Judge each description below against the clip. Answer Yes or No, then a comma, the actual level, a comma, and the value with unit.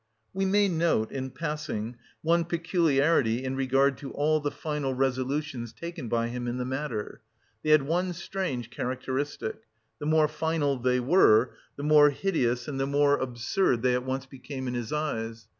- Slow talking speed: No, average, 170 wpm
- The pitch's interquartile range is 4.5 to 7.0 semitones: No, average, 3.7 semitones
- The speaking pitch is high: No, low, 135 Hz